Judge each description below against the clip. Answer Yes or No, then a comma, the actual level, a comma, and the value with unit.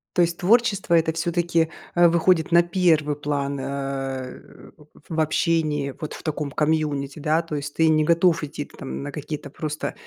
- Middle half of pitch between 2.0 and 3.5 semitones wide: Yes, average, 2.8 semitones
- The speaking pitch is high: No, medium, 155 Hz